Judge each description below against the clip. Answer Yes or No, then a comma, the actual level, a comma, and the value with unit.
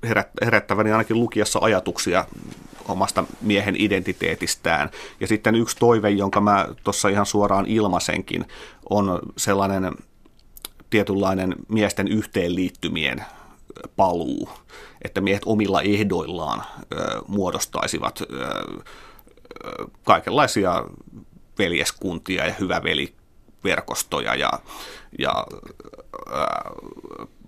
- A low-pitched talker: Yes, low, 100 Hz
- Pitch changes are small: Yes, narrow, 1.7 semitones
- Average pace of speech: No, slow, 75 wpm